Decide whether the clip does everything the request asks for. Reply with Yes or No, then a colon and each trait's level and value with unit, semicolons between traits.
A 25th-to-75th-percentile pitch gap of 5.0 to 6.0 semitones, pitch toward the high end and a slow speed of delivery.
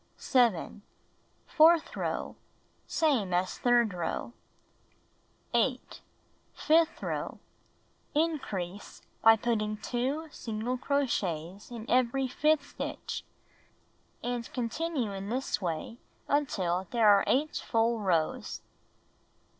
Yes: wide, 5.4 semitones; high, 235 Hz; slow, 100 wpm